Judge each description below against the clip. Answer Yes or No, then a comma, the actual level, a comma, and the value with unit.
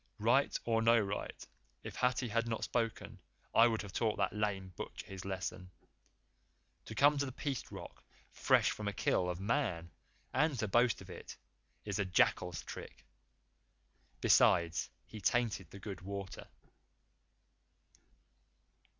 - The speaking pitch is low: Yes, low, 105 Hz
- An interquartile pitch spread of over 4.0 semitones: No, average, 3.5 semitones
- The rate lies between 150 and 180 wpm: No, average, 140 wpm